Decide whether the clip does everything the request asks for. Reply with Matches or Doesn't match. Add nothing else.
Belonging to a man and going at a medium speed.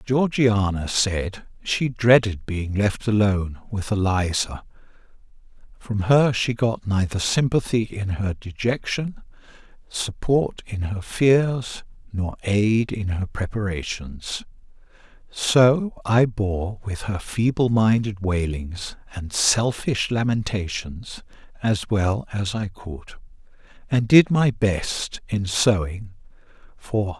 Doesn't match